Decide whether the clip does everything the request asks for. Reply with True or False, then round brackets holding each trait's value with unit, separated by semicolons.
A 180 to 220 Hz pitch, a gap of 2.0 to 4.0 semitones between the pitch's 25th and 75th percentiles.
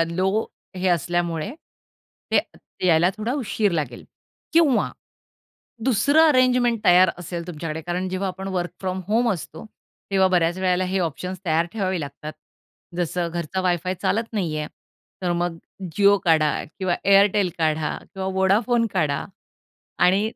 True (185 Hz; 3.0 semitones)